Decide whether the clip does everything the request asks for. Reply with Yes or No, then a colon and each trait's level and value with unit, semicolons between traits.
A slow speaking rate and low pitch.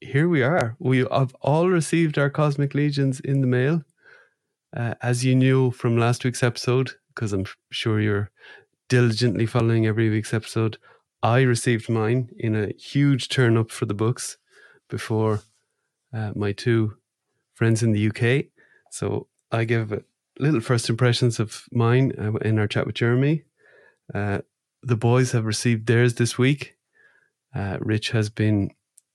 No: average, 155 wpm; low, 120 Hz